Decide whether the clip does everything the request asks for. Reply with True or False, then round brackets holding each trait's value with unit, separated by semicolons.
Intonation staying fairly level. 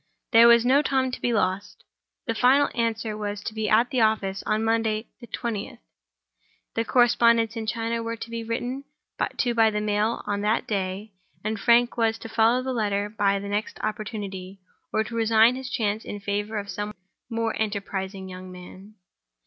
True (2.1 semitones)